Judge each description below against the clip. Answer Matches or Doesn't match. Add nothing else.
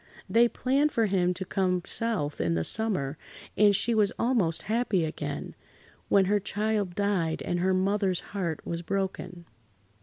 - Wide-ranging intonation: Doesn't match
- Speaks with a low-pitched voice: Doesn't match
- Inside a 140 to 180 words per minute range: Matches